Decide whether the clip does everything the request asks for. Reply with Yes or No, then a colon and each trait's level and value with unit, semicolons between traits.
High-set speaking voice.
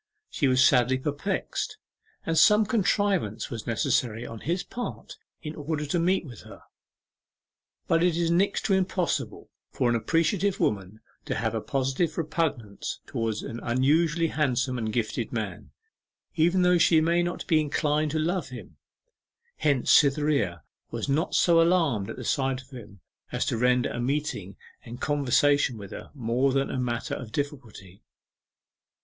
No: medium, 140 Hz